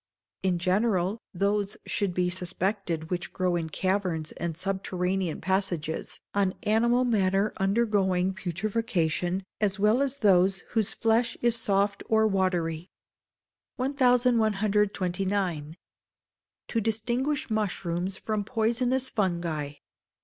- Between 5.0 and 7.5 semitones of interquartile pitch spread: No, average, 3.5 semitones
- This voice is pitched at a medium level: No, high, 195 Hz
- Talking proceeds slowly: Yes, slow, 105 wpm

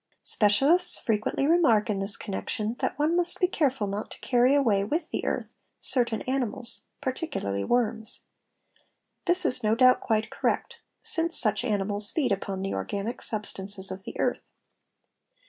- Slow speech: No, average, 150 wpm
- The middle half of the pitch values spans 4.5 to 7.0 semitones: Yes, average, 5.0 semitones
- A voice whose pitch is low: No, high, 225 Hz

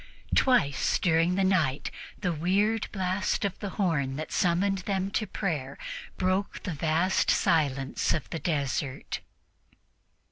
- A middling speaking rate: No, slow, 130 wpm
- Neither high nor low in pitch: Yes, medium, 180 Hz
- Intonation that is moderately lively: Yes, average, 4.2 semitones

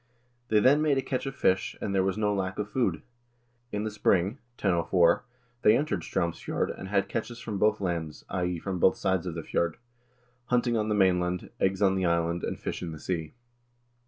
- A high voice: No, very low, 95 Hz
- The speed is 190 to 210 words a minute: Yes, average, 200 wpm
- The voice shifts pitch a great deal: No, average, 3.4 semitones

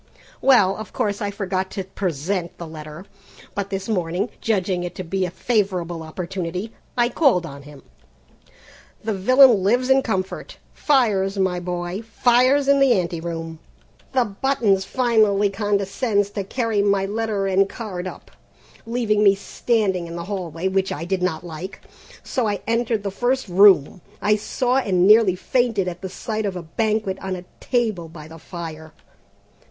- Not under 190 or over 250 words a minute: No, average, 165 wpm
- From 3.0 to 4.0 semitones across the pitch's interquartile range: Yes, average, 3.7 semitones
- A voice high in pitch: Yes, high, 195 Hz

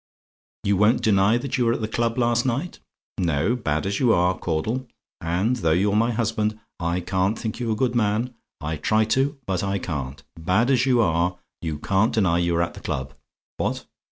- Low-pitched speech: Yes, low, 105 Hz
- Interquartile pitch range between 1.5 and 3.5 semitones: No, average, 5.3 semitones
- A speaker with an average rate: No, fast, 210 wpm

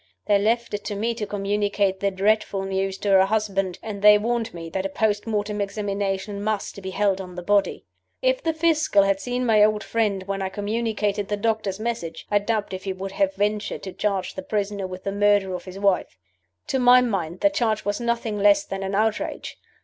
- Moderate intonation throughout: No, narrow, 1.9 semitones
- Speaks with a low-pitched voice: No, high, 205 Hz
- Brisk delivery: Yes, fast, 210 wpm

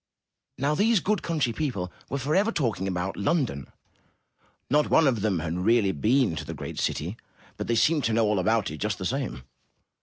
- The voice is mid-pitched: No, low, 115 Hz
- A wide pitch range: Yes, wide, 8.2 semitones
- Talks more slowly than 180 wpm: No, average, 190 wpm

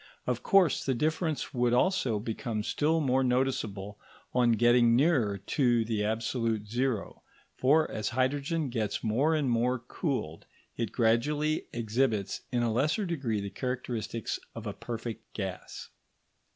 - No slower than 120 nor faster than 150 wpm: Yes, average, 140 wpm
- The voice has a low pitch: Yes, low, 120 Hz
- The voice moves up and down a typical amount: Yes, average, 3.5 semitones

